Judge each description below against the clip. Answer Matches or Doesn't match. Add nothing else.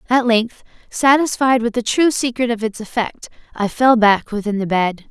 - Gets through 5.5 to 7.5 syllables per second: Doesn't match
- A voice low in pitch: Doesn't match